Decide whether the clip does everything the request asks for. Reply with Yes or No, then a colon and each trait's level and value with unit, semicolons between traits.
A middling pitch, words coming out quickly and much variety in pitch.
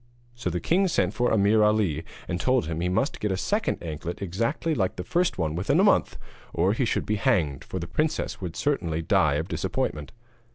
No: very low, 95 Hz; fast, 210 wpm; wide, 6.3 semitones